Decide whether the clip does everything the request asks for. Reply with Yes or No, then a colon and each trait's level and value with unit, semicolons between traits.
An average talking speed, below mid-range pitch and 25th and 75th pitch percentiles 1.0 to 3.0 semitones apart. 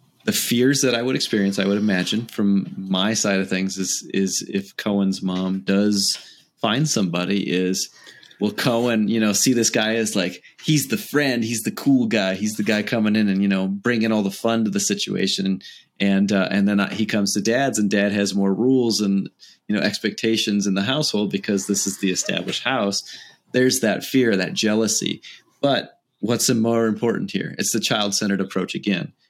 Yes: average, 195 wpm; low, 105 Hz; narrow, 2.4 semitones